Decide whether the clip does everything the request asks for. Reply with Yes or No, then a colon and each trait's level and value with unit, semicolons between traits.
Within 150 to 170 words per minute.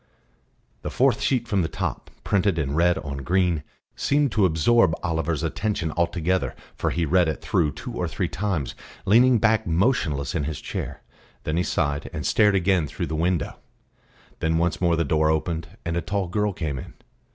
No: average, 185 wpm